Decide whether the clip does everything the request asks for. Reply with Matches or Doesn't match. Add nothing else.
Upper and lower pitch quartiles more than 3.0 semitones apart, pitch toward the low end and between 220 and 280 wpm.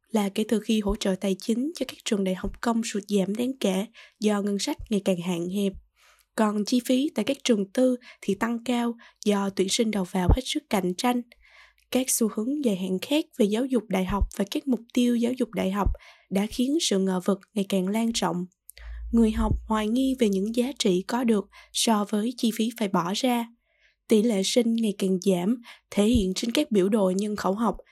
Doesn't match